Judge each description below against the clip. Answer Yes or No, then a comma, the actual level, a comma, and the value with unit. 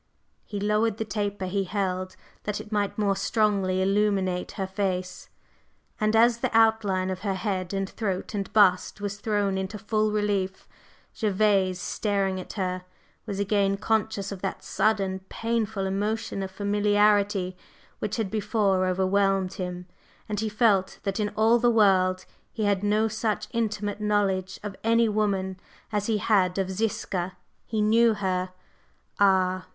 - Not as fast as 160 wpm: Yes, average, 150 wpm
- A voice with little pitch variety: Yes, narrow, 2.0 semitones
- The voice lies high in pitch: Yes, high, 200 Hz